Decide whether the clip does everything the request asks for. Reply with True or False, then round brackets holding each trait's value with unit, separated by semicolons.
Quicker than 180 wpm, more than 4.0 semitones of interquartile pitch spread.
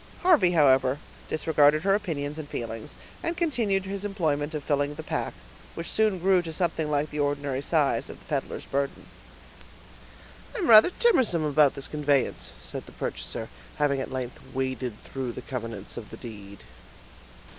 False (160 wpm; 5.0 semitones)